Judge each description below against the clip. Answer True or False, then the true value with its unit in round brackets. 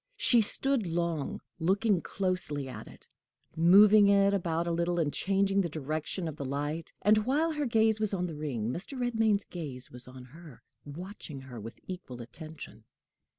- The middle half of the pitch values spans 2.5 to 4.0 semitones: False (5.5 semitones)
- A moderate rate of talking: True (170 wpm)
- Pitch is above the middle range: False (170 Hz)